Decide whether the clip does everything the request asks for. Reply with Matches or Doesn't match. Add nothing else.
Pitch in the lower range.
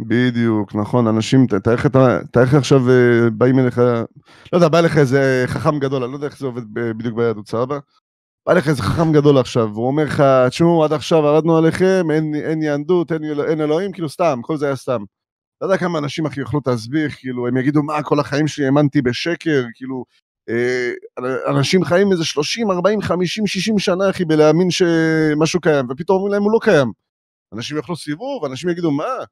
Doesn't match